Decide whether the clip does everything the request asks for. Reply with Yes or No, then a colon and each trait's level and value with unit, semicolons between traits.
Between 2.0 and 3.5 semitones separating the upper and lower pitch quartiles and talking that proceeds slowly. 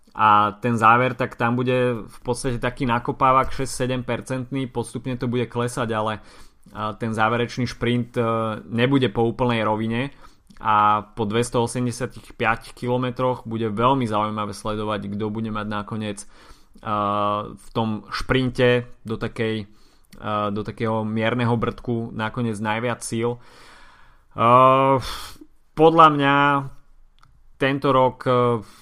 Yes: average, 2.7 semitones; slow, 105 wpm